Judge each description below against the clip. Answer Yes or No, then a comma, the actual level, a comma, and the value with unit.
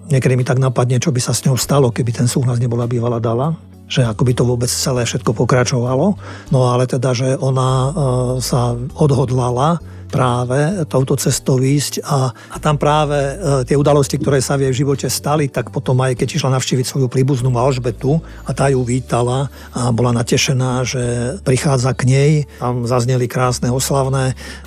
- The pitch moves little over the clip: Yes, narrow, 2.1 semitones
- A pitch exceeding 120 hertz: Yes, low, 130 Hz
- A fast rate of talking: Yes, fast, 175 wpm